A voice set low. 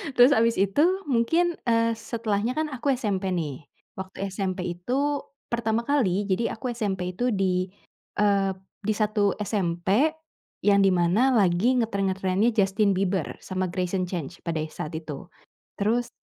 No: high, 200 Hz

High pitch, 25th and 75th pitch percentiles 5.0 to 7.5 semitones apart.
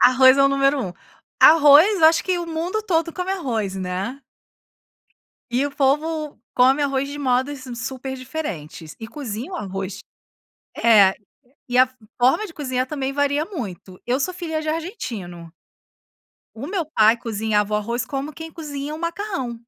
Yes: very high, 275 Hz; wide, 5.5 semitones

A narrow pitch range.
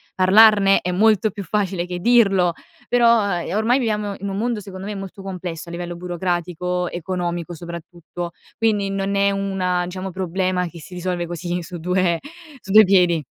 Yes: narrow, 2.2 semitones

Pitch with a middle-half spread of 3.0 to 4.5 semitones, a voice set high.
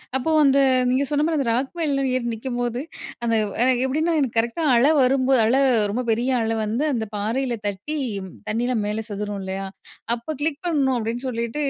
Yes: average, 3.5 semitones; very high, 250 Hz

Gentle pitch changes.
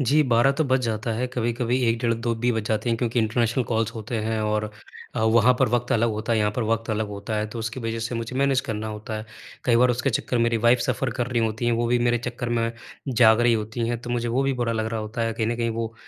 Yes: narrow, 1.5 semitones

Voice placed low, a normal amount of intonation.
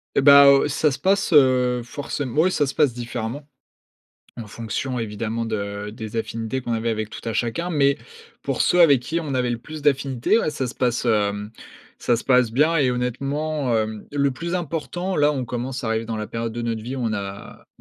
Yes: low, 125 Hz; average, 4.1 semitones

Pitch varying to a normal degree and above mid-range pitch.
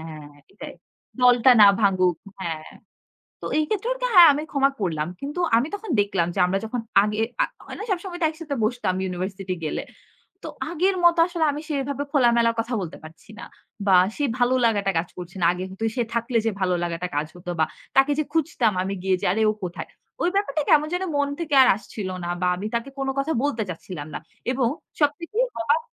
No: wide, 8.1 semitones; high, 235 Hz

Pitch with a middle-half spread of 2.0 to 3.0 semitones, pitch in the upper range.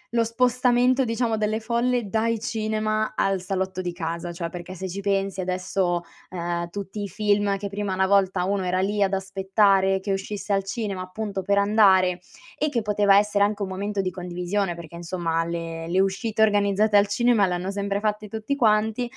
Yes: narrow, 2.6 semitones; high, 200 Hz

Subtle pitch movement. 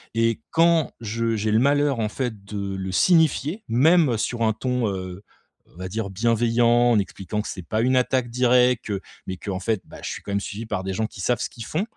No: average, 3.7 semitones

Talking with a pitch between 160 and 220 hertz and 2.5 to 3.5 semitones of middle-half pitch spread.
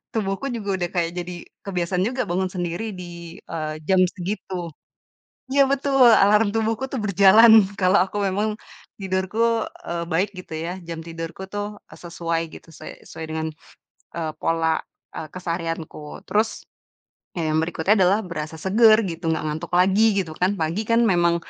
No: medium, 185 Hz; average, 3.9 semitones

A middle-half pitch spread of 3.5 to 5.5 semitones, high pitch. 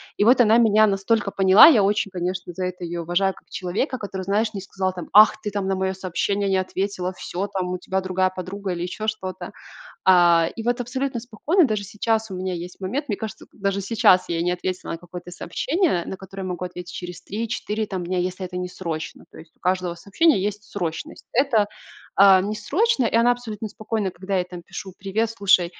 No: average, 2.9 semitones; high, 195 Hz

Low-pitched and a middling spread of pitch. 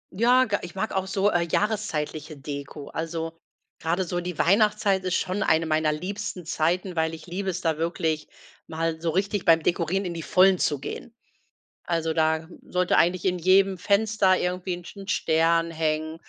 No: medium, 175 Hz; average, 3.0 semitones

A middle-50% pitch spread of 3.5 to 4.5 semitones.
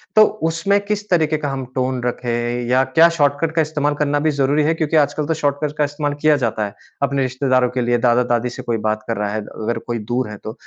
Yes: average, 4.0 semitones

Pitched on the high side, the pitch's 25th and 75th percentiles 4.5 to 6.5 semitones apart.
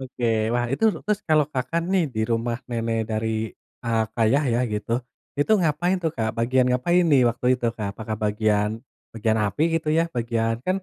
No: low, 120 Hz; average, 4.8 semitones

